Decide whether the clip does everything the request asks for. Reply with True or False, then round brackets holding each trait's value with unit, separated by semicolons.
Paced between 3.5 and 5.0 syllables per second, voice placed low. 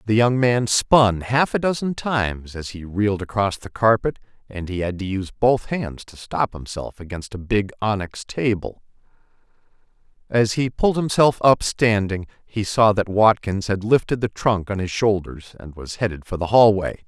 True (4.8 syllables/s; 105 Hz)